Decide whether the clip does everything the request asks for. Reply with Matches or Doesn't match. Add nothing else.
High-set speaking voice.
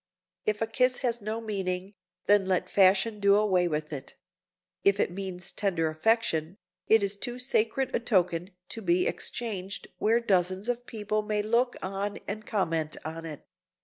Matches